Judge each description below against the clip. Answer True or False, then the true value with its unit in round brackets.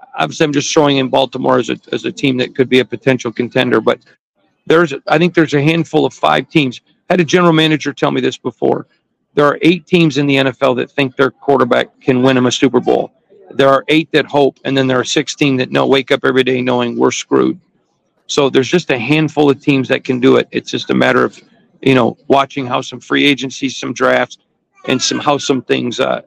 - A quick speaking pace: True (240 wpm)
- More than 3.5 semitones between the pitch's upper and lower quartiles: False (2.8 semitones)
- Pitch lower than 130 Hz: False (135 Hz)